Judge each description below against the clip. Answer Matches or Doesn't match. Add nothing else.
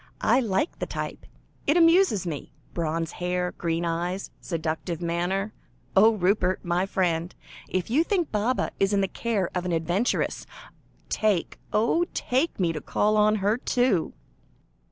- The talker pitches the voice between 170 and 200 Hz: Matches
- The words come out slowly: Doesn't match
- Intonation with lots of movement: Doesn't match